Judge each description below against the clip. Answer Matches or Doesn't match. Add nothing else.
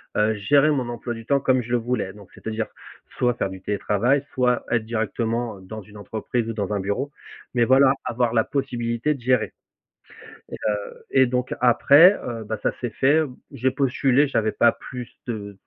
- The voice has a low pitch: Matches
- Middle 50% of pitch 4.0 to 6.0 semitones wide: Doesn't match